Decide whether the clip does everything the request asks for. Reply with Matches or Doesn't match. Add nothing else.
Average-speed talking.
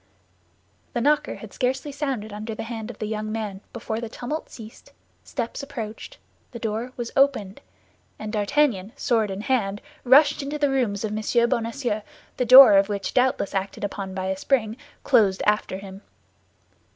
Matches